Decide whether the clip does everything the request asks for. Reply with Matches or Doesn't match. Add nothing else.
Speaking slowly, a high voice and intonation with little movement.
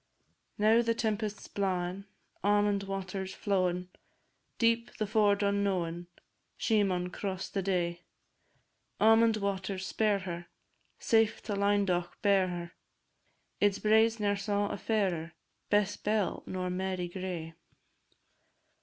Matches